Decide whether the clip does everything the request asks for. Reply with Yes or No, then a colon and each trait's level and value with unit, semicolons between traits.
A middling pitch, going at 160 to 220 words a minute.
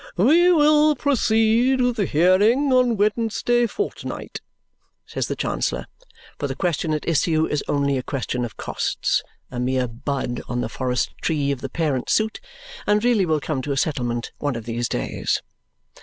Yes: medium, 160 Hz; average, 170 wpm